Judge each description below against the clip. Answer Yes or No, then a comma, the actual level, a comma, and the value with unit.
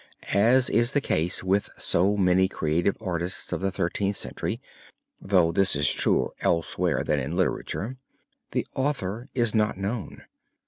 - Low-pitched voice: Yes, very low, 95 Hz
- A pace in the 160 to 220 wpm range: No, average, 145 wpm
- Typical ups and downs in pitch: Yes, average, 3.8 semitones